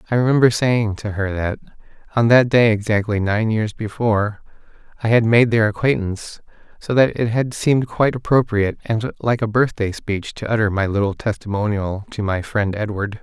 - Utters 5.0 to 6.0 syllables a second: Yes, 5.3 syllables/s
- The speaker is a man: Yes, male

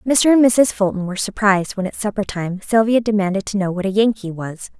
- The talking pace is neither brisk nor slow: No, fast, 225 wpm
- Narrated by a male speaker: No, female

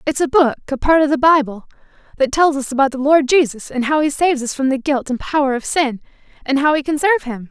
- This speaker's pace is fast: Yes, fast, 250 wpm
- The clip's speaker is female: Yes, female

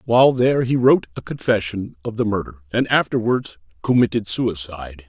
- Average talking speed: Yes, average, 155 wpm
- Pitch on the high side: No, low, 110 Hz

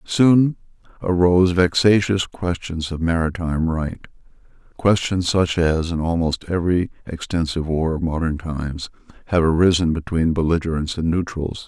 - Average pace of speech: No, slow, 125 wpm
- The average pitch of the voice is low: Yes, very low, 85 Hz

